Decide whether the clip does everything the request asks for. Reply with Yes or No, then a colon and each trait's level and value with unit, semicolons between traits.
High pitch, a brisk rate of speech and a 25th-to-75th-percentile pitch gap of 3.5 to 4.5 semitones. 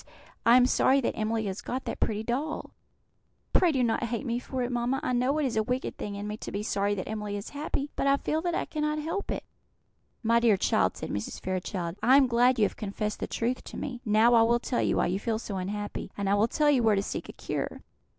Yes: high, 235 Hz; fast, 250 wpm; average, 4.0 semitones